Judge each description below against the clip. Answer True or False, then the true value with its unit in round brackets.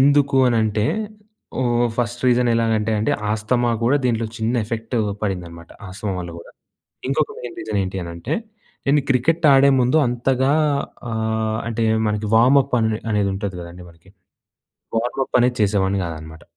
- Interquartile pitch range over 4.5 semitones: False (3.6 semitones)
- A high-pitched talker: False (115 Hz)